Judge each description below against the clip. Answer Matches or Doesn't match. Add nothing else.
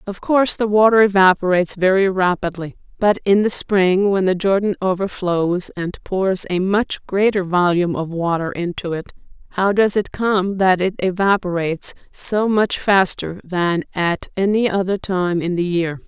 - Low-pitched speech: Doesn't match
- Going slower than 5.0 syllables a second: Matches